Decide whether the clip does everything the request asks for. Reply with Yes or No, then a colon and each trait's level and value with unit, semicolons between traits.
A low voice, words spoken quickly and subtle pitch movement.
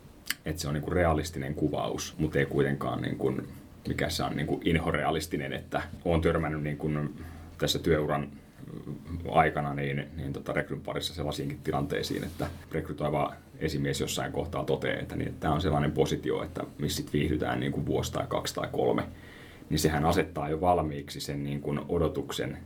Yes: very low, 75 Hz; fast, 160 wpm; narrow, 2.1 semitones